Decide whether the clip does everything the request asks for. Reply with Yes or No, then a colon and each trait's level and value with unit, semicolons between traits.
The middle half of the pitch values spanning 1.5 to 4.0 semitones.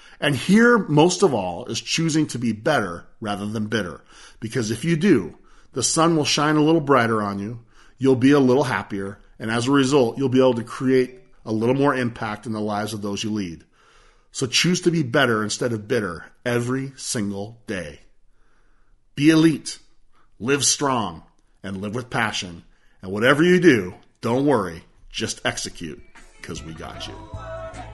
No: average, 5.0 semitones